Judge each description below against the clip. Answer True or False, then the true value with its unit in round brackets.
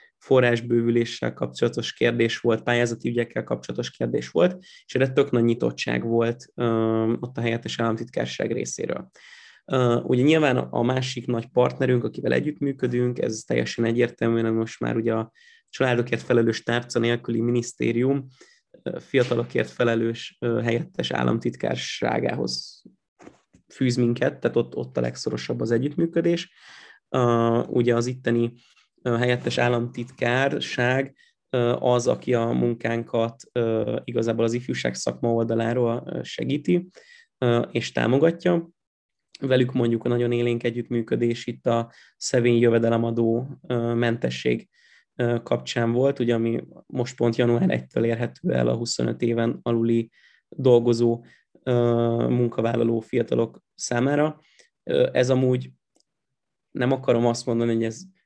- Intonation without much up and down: True (1.5 semitones)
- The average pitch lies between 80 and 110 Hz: False (120 Hz)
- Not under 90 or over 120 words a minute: True (110 wpm)